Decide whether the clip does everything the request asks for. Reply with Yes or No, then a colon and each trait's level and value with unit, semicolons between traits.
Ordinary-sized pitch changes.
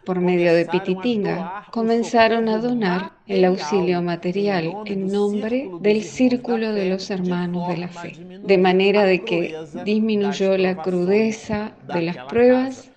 Yes: average, 3.4 semitones